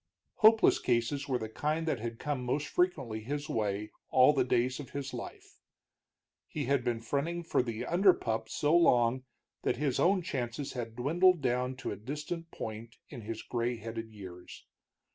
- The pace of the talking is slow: No, average, 175 wpm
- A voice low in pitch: Yes, low, 125 Hz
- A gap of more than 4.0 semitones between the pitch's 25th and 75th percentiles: Yes, average, 4.4 semitones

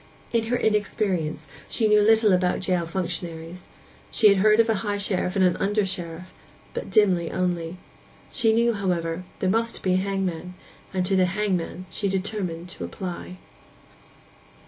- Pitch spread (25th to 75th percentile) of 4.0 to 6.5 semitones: No, average, 2.9 semitones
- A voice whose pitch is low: No, medium, 185 Hz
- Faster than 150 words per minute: Yes, average, 165 wpm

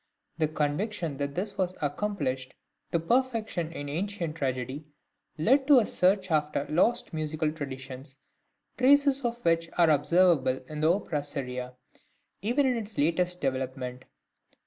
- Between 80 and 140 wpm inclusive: Yes, slow, 135 wpm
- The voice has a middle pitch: Yes, medium, 160 Hz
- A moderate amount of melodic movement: No, wide, 6.2 semitones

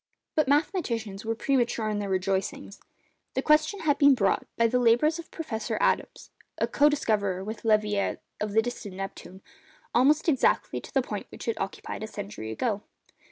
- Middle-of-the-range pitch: No, high, 225 Hz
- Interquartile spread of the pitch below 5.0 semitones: No, wide, 5.5 semitones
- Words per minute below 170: Yes, average, 160 wpm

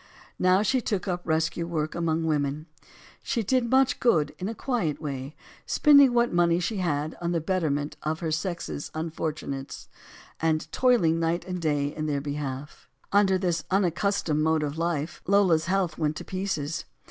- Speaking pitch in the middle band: Yes, medium, 165 Hz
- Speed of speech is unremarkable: Yes, average, 170 wpm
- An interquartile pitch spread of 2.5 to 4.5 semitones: Yes, average, 3.7 semitones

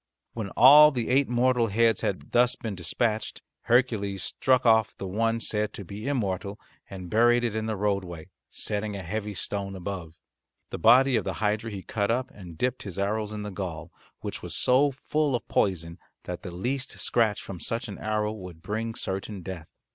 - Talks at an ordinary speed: Yes, average, 190 wpm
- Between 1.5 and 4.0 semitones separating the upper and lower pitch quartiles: Yes, average, 3.4 semitones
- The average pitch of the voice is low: Yes, low, 105 Hz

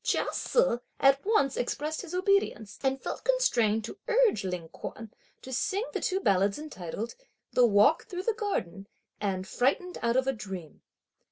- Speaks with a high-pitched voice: Yes, very high, 260 Hz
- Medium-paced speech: Yes, average, 165 wpm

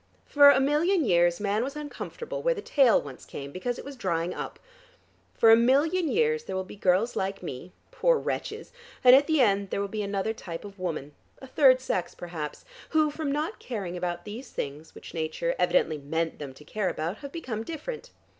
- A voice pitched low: No, high, 215 Hz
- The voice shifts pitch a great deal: Yes, wide, 8.4 semitones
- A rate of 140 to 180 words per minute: No, average, 200 wpm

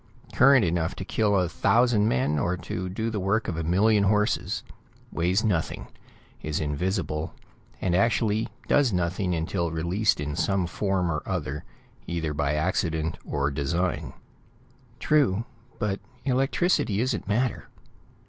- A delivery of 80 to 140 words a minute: Yes, slow, 135 wpm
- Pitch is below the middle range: Yes, very low, 90 Hz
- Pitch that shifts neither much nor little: Yes, average, 4.8 semitones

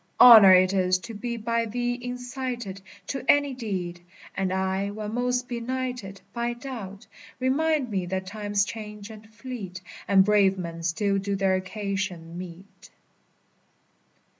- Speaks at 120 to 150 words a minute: Yes, average, 140 wpm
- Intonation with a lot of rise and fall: No, average, 4.2 semitones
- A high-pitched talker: Yes, high, 205 Hz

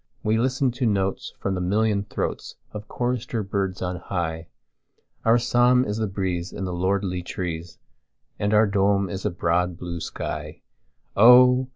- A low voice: Yes, low, 100 Hz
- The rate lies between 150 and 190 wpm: No, average, 140 wpm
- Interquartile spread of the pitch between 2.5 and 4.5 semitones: Yes, average, 3.9 semitones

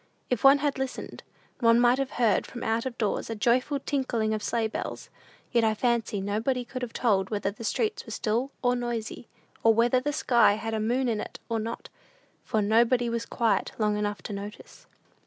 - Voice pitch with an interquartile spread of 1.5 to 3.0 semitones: Yes, narrow, 2.4 semitones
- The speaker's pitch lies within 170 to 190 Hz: No, high, 230 Hz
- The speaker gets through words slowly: No, average, 200 wpm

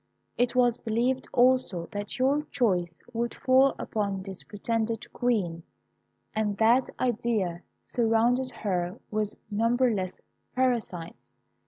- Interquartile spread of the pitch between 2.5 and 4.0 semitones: Yes, average, 3.7 semitones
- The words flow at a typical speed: No, slow, 110 wpm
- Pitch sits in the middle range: No, high, 225 Hz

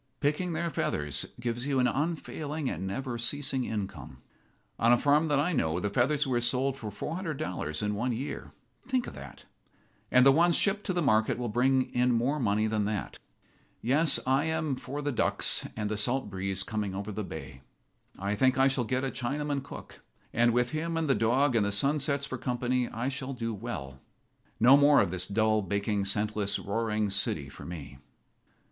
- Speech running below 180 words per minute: No, average, 190 wpm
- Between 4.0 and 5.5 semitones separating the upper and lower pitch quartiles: Yes, average, 5.1 semitones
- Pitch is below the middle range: Yes, low, 125 Hz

